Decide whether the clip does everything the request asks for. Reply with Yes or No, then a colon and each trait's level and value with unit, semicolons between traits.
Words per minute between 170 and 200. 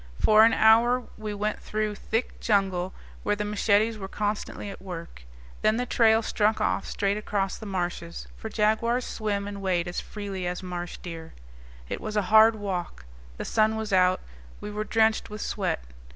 Yes: average, 180 wpm